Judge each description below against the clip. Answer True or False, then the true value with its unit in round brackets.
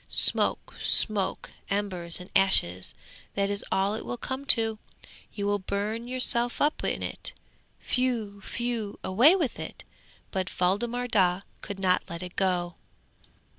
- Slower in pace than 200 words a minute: True (140 wpm)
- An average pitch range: True (4.2 semitones)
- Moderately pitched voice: False (205 Hz)